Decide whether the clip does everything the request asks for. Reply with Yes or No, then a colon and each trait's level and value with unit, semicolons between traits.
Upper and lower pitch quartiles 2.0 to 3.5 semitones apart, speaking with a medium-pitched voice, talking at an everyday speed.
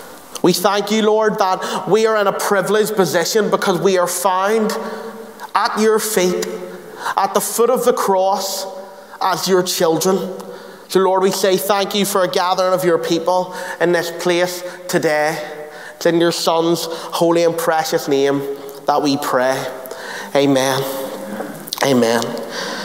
Yes: average, 3.0 semitones; medium, 180 Hz; average, 145 wpm